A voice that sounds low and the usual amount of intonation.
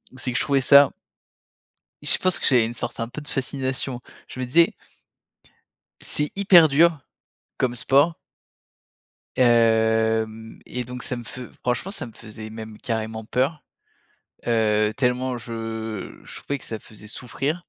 Yes: low, 125 Hz; average, 3.6 semitones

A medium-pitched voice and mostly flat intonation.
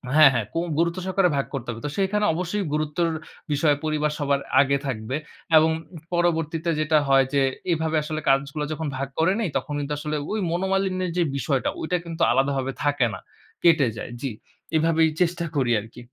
No: medium, 155 Hz; average, 3.6 semitones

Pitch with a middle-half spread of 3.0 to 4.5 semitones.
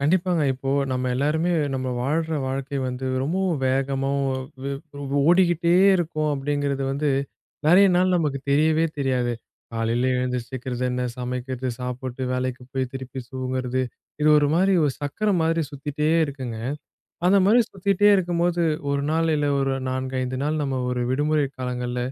Yes: average, 3.9 semitones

